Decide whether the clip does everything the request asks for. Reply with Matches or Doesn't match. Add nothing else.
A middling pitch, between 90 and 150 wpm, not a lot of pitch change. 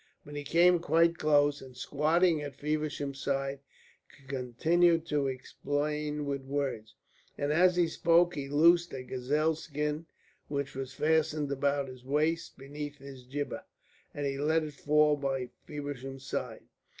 Matches